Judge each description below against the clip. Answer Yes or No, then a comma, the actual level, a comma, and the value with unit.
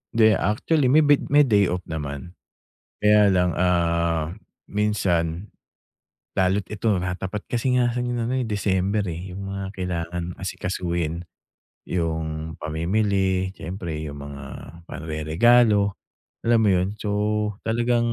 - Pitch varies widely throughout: No, average, 4.2 semitones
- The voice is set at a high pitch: No, very low, 95 Hz